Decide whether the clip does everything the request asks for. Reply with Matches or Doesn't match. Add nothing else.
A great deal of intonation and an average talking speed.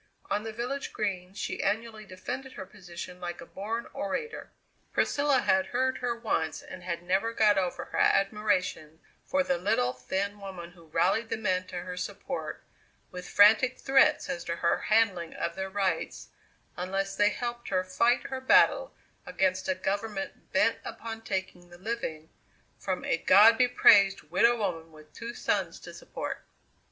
Doesn't match